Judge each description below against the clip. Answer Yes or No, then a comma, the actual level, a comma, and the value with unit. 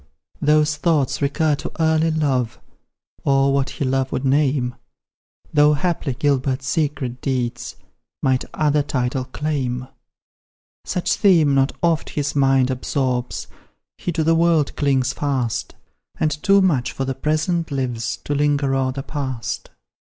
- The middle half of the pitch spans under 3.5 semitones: Yes, average, 2.8 semitones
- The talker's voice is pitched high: No, medium, 140 Hz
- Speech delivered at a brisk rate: No, slow, 135 wpm